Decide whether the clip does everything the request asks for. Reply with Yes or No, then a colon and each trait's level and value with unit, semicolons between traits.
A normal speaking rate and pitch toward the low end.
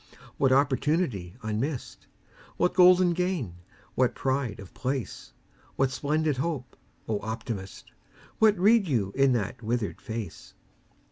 No: slow, 120 wpm; low, 130 Hz